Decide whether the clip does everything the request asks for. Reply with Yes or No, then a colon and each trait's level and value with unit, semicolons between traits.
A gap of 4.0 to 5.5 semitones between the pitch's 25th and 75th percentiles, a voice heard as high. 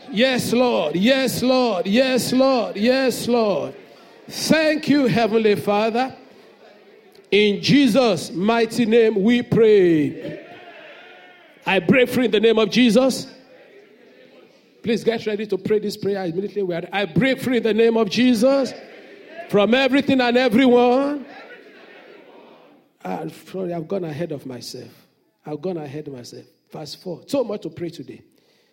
Yes: average, 4.7 semitones; high, 230 Hz